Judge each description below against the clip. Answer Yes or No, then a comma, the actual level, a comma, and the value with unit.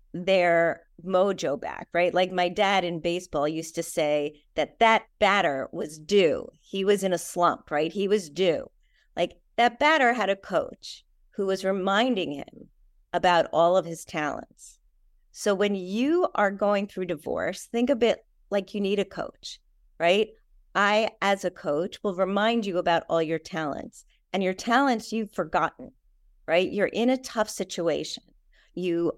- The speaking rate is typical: Yes, average, 165 wpm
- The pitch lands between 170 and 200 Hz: Yes, high, 190 Hz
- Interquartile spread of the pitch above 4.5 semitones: No, average, 3.3 semitones